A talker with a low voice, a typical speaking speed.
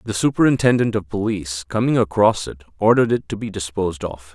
Yes: low, 100 Hz; average, 180 wpm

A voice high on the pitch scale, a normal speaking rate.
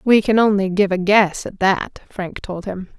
No: high, 195 Hz; fast, 220 wpm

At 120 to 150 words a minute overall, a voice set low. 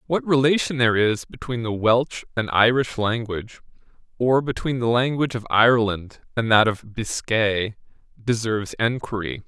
Yes: average, 140 wpm; low, 115 Hz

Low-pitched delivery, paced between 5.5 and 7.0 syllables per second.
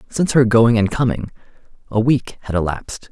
Yes: low, 115 Hz; 5.8 syllables/s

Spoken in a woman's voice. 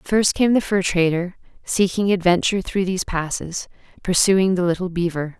Yes: female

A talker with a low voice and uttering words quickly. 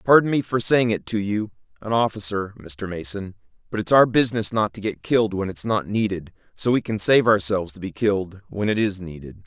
Yes: low, 100 Hz; fast, 220 wpm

